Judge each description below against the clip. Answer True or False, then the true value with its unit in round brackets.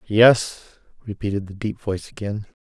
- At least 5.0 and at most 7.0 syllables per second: False (4.8 syllables/s)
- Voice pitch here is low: True (105 Hz)